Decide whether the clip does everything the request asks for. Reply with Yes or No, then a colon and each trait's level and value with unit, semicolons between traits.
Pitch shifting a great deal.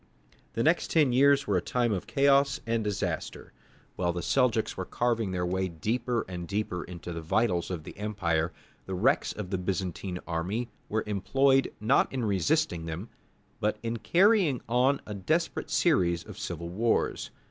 Yes: wide, 6.0 semitones